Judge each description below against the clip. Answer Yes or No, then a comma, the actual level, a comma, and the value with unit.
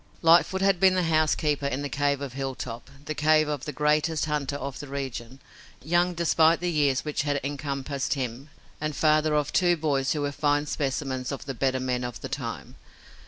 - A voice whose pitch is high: No, medium, 145 Hz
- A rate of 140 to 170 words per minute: No, average, 195 wpm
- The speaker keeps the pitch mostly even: Yes, narrow, 2.3 semitones